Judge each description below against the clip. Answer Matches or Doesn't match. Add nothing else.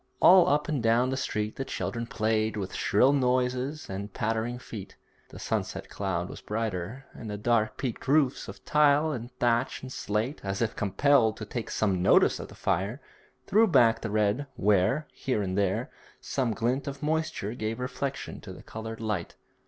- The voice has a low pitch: Matches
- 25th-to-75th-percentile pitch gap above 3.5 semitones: Matches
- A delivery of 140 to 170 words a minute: Doesn't match